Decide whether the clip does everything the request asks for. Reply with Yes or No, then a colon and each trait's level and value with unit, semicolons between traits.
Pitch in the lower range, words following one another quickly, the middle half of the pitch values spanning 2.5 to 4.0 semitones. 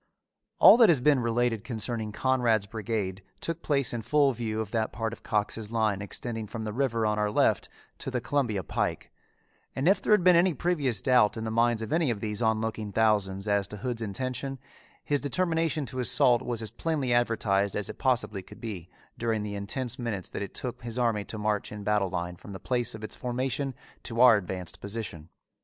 Yes: low, 115 Hz; fast, 210 wpm; average, 3.4 semitones